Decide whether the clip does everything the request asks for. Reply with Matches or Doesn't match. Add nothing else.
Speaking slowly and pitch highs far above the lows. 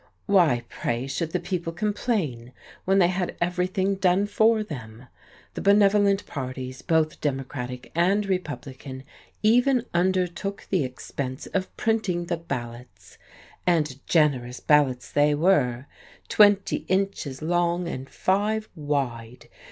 Matches